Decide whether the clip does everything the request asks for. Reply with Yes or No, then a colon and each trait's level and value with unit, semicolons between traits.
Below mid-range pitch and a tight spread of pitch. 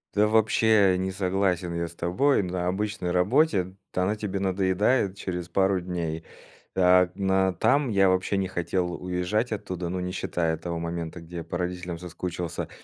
Yes: very low, 90 Hz; narrow, 1.9 semitones